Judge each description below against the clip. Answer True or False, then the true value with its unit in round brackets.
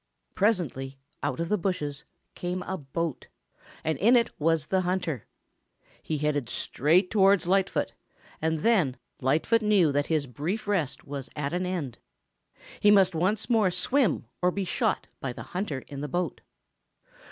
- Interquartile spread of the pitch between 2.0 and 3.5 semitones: False (5.0 semitones)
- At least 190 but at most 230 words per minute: False (155 wpm)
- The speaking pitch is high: False (170 Hz)